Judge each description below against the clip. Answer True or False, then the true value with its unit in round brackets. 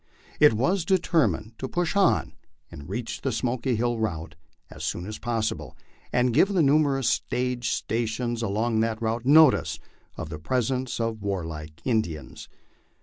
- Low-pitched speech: True (115 Hz)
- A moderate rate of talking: True (145 wpm)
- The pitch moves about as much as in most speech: True (3.4 semitones)